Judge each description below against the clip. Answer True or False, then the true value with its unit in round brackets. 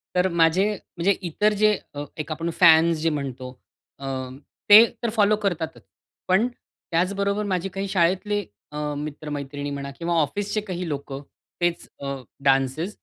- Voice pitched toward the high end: False (170 Hz)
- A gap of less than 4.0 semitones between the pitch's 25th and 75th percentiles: False (5.3 semitones)